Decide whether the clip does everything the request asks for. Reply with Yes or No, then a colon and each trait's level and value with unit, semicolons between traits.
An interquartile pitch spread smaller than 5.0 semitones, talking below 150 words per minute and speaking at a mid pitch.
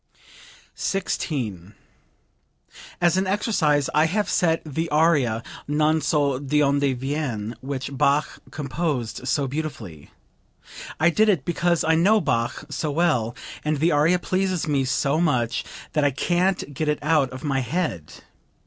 Yes: average, 4.0 semitones; average, 140 wpm; medium, 150 Hz